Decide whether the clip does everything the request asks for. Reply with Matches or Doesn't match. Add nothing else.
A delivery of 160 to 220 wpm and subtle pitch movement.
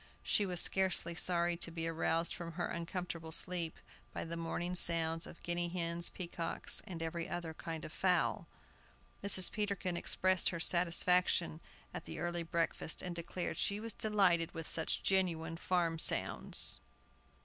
Doesn't match